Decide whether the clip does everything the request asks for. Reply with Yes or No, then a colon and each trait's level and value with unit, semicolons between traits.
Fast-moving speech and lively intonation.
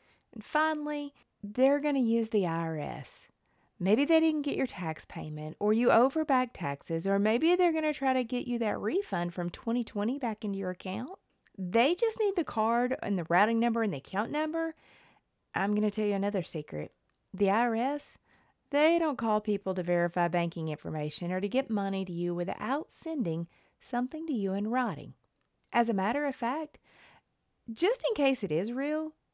No: average, 185 wpm; wide, 6.9 semitones